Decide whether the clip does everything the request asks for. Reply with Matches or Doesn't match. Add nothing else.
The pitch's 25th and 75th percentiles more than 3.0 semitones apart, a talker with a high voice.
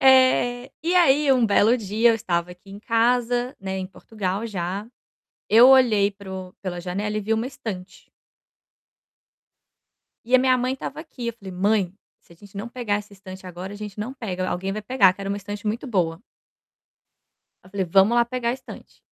Matches